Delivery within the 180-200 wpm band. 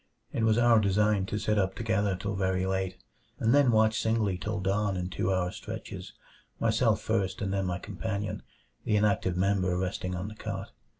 Yes: average, 185 wpm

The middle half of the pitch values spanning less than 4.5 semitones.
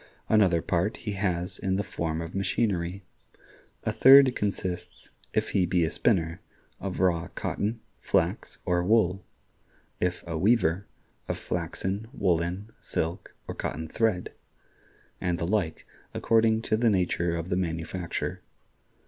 Yes: average, 3.4 semitones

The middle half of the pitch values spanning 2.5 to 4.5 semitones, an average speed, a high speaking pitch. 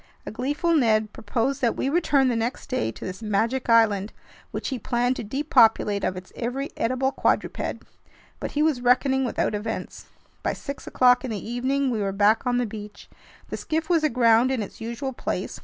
Yes: average, 3.3 semitones; average, 190 wpm; high, 245 Hz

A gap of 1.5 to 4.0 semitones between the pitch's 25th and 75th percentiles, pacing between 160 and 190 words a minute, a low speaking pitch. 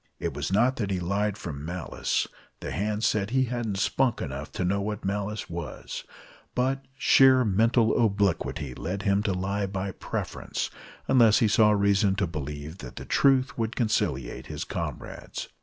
Yes: average, 3.4 semitones; average, 165 wpm; low, 100 Hz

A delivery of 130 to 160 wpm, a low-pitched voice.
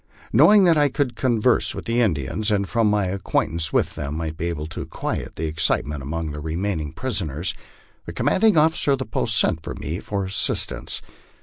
No: average, 195 wpm; very low, 95 Hz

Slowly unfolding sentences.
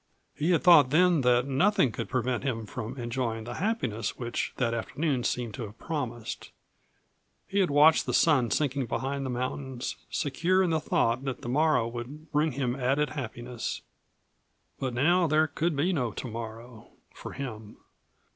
No: average, 165 wpm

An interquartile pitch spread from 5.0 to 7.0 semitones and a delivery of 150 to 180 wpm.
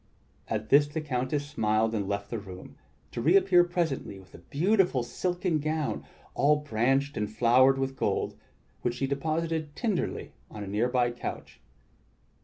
Yes: average, 5.3 semitones; average, 160 wpm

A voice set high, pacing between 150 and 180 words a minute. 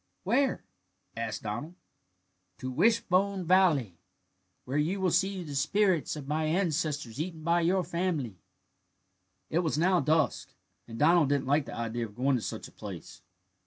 No: medium, 155 Hz; average, 155 wpm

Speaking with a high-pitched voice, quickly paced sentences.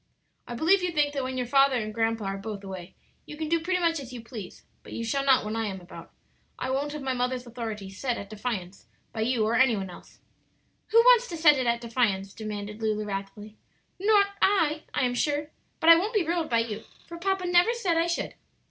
Yes: very high, 250 Hz; fast, 230 wpm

